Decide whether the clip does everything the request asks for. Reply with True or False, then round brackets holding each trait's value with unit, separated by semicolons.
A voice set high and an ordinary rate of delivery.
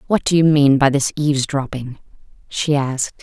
False (140 Hz; 165 wpm)